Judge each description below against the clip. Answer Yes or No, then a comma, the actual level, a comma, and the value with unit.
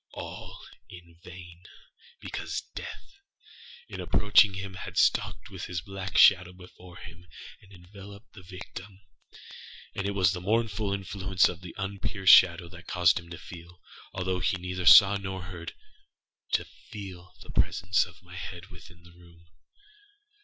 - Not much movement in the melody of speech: Yes, narrow, 1.8 semitones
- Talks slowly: No, average, 145 wpm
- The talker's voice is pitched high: No, very low, 90 Hz